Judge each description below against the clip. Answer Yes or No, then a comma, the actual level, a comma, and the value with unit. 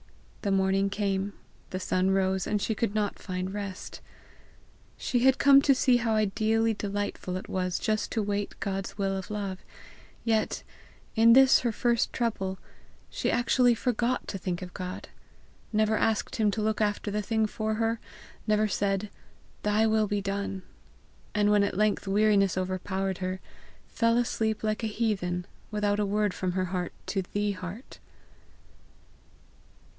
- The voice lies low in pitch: No, high, 205 Hz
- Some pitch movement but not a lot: No, narrow, 2.2 semitones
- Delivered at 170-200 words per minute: No, average, 160 wpm